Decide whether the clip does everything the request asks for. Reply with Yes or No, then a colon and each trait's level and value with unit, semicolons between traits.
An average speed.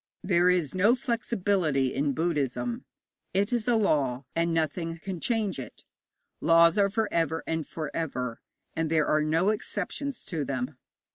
Yes: average, 155 wpm